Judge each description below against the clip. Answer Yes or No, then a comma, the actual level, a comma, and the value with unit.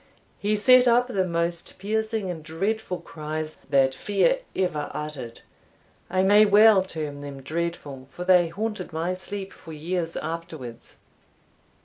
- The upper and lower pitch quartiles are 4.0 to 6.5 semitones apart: Yes, average, 4.8 semitones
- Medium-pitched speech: Yes, medium, 175 Hz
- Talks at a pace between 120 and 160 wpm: Yes, slow, 135 wpm